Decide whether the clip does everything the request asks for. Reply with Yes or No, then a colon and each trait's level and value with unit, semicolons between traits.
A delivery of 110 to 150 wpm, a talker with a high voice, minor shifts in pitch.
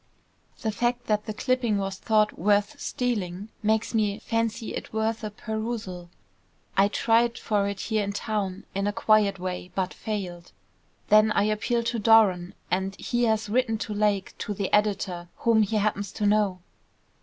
No: average, 165 wpm; high, 210 Hz; narrow, 2.1 semitones